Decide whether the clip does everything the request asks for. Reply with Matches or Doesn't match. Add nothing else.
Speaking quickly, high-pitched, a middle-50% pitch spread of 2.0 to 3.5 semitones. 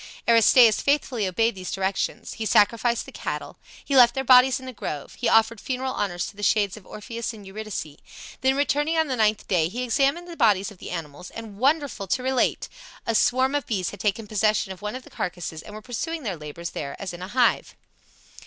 Doesn't match